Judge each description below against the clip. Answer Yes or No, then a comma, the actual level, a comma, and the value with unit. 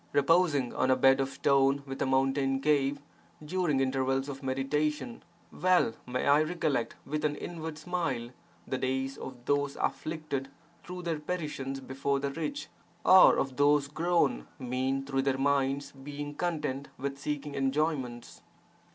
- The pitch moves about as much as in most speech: No, narrow, 2.2 semitones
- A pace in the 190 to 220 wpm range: No, average, 145 wpm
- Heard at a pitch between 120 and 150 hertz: Yes, medium, 140 Hz